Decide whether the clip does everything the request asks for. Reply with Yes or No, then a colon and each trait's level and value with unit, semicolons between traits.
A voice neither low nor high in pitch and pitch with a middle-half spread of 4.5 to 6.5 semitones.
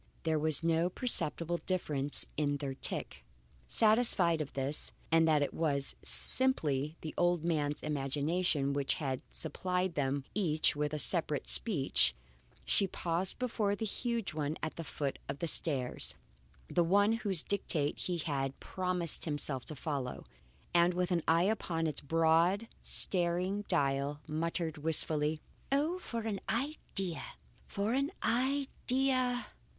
Yes: medium, 165 Hz; average, 5.0 semitones